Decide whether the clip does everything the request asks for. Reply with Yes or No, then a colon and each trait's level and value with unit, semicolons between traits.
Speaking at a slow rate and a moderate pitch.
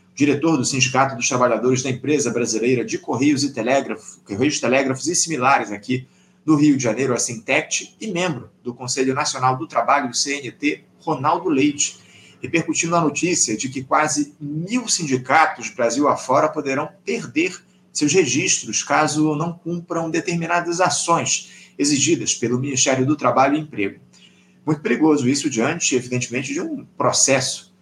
No: average, 145 wpm; medium, 145 Hz